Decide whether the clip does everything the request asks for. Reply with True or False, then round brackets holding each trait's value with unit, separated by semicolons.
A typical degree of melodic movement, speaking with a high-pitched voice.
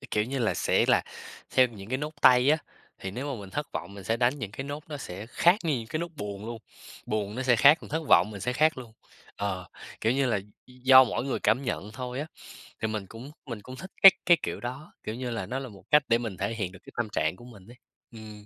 False (4.2 semitones; 120 Hz)